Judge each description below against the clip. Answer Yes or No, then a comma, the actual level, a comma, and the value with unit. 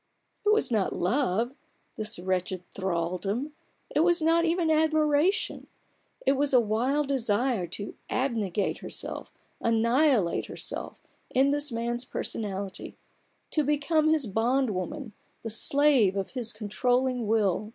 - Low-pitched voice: No, high, 240 Hz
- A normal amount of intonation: No, wide, 5.9 semitones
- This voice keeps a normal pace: No, slow, 125 wpm